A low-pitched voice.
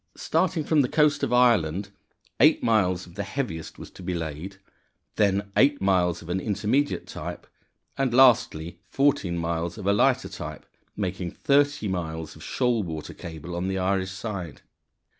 Yes: very low, 95 Hz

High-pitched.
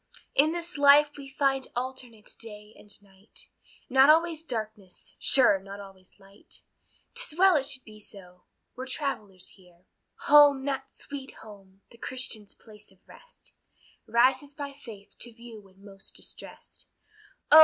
Yes: high, 240 Hz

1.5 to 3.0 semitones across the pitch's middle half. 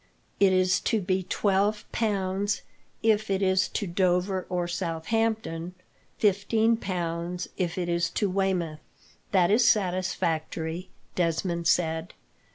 Yes: average, 2.7 semitones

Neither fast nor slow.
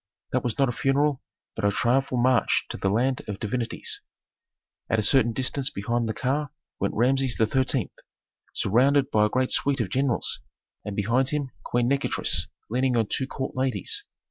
Yes: average, 170 wpm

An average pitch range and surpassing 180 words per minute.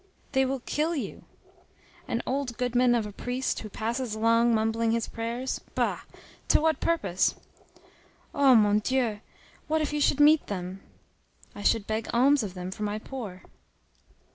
No: average, 3.8 semitones; average, 160 wpm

